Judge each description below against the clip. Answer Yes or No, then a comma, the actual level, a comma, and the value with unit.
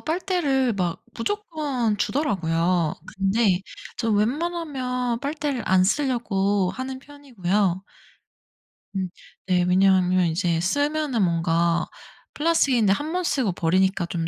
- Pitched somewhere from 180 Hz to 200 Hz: No, high, 210 Hz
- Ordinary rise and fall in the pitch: No, wide, 7.5 semitones